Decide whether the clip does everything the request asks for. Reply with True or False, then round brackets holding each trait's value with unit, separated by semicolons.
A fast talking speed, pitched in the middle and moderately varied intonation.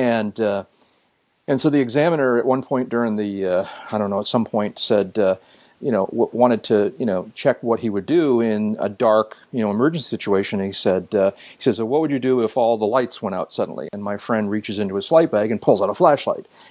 False (250 wpm; 110 Hz; 3.7 semitones)